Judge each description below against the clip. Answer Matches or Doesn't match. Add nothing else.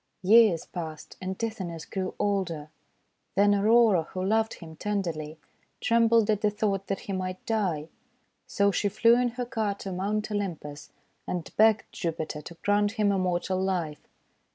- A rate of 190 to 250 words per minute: Doesn't match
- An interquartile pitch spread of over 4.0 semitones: Doesn't match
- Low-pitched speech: Doesn't match